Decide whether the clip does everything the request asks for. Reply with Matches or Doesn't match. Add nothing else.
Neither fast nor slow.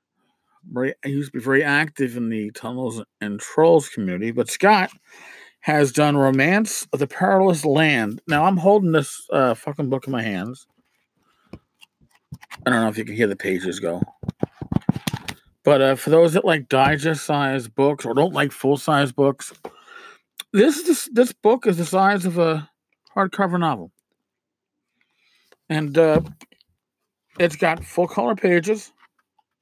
Matches